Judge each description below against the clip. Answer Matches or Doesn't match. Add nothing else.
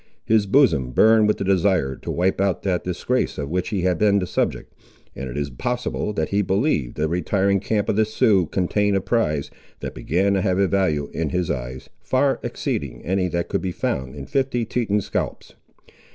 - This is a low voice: Matches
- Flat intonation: Doesn't match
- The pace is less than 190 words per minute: Doesn't match